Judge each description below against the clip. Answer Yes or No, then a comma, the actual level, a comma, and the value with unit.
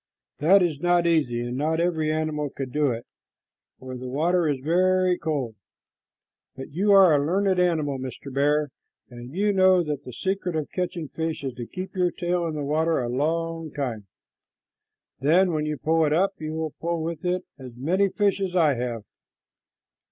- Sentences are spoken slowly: No, average, 185 wpm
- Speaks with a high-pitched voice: No, medium, 160 Hz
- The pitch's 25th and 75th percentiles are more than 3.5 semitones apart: Yes, average, 4.2 semitones